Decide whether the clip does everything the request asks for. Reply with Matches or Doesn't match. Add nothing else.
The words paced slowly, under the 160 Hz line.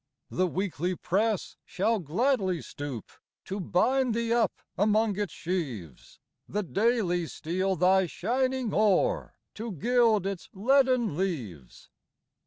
Doesn't match